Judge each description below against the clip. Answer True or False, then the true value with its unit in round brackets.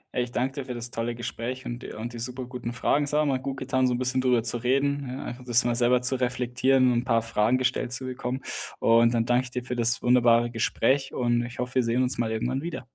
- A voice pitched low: True (125 Hz)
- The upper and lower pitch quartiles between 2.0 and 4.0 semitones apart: False (1.4 semitones)